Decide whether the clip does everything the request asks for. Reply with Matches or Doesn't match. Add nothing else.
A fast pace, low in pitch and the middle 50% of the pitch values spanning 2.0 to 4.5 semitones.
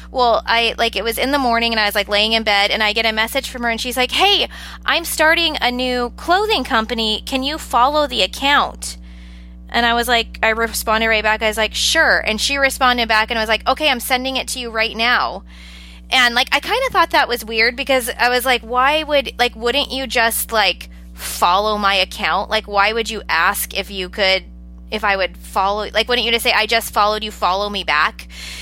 Doesn't match